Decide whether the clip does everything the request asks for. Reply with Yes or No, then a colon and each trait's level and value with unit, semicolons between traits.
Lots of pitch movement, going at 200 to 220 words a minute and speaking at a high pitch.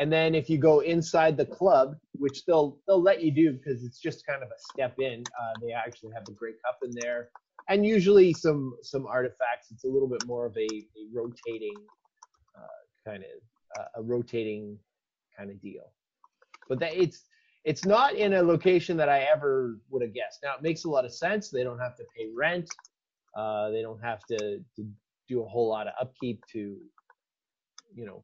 No: wide, 6.9 semitones; fast, 205 wpm; low, 135 Hz